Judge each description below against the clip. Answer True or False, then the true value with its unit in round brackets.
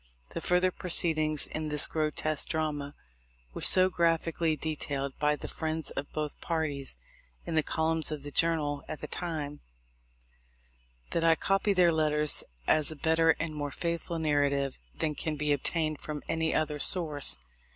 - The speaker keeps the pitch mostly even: True (1.8 semitones)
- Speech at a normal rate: True (160 wpm)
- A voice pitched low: False (155 Hz)